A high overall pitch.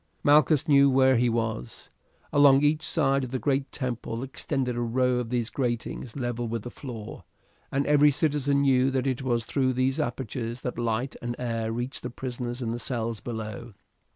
No: low, 125 Hz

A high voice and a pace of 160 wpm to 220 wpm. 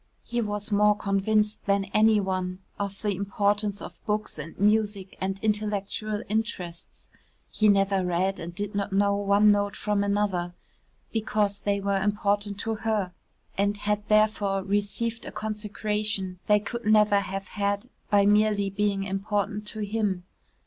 No: high, 205 Hz; average, 150 wpm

